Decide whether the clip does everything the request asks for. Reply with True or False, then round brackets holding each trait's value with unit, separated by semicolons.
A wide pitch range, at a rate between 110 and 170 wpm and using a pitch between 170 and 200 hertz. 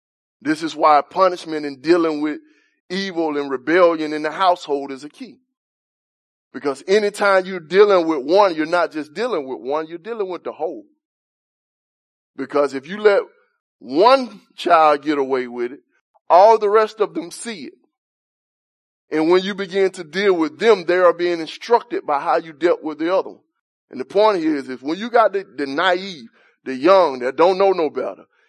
False (6.9 semitones; 185 wpm; 185 Hz)